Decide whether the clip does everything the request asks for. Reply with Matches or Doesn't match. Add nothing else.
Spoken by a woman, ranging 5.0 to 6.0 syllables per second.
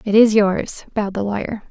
Matches